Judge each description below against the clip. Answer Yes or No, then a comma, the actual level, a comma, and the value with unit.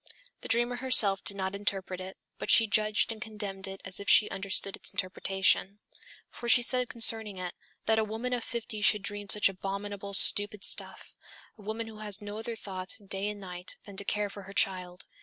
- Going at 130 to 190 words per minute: No, average, 200 wpm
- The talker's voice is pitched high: Yes, high, 205 Hz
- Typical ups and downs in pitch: No, narrow, 2.3 semitones